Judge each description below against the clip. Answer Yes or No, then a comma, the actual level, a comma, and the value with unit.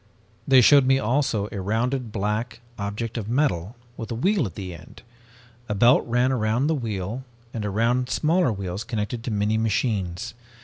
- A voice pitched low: Yes, low, 115 Hz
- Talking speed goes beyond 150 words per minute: Yes, average, 170 wpm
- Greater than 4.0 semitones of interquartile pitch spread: No, average, 3.5 semitones